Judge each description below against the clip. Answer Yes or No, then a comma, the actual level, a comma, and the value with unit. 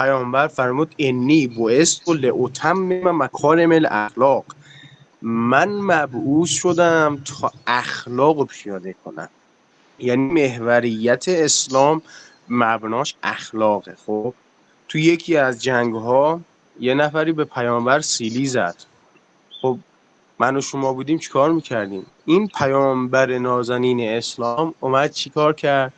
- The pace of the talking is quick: No, average, 115 wpm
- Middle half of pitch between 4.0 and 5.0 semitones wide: Yes, average, 4.4 semitones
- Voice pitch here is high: No, low, 135 Hz